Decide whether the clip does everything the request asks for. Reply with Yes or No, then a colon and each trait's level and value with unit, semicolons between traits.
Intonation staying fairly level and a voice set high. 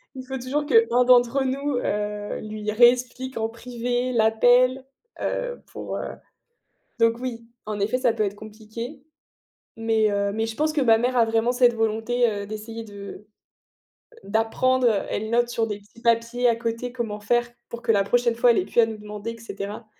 Yes: narrow, 2.3 semitones; high, 230 Hz